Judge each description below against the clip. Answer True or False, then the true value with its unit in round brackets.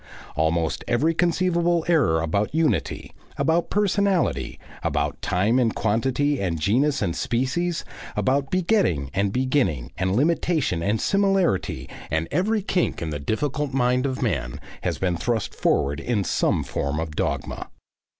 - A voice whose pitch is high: False (125 Hz)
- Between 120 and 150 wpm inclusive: True (140 wpm)